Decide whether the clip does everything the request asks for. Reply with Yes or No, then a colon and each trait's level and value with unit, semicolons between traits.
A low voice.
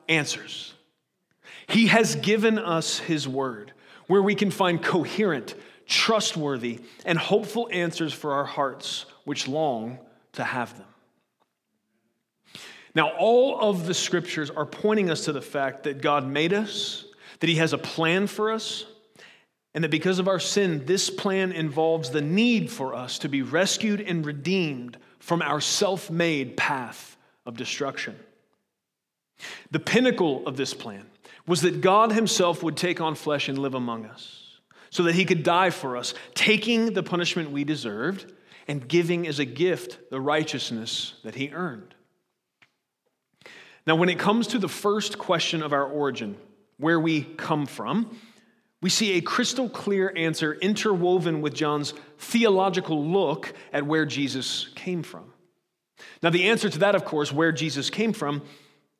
No: medium, 170 Hz